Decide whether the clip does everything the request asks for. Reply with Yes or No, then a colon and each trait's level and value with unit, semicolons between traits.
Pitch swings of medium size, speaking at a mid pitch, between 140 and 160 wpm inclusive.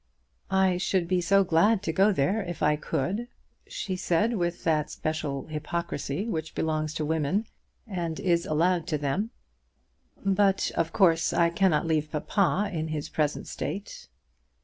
Yes: average, 3.6 semitones; medium, 170 Hz; average, 150 wpm